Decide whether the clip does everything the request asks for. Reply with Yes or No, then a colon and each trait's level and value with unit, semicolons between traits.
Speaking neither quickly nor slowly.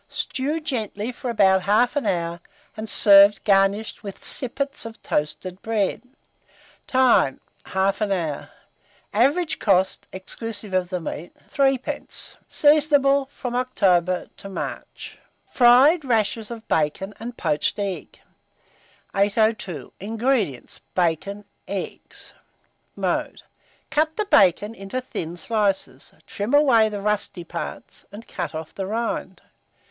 No: slow, 115 wpm